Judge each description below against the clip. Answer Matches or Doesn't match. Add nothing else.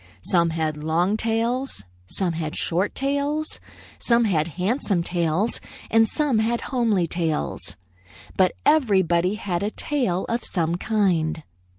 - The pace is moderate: Doesn't match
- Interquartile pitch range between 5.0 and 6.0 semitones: Matches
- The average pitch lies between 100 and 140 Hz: Doesn't match